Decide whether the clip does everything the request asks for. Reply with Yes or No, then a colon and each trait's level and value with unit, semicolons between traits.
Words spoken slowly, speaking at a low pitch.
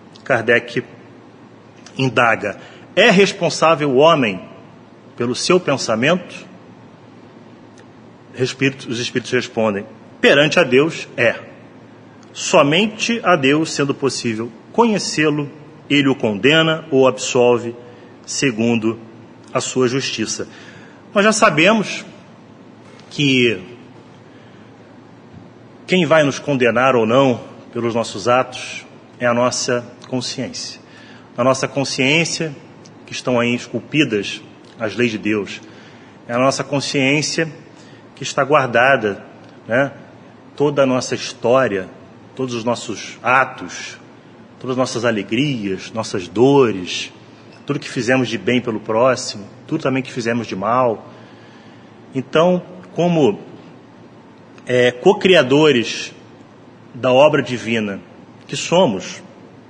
Yes: slow, 105 wpm; low, 130 Hz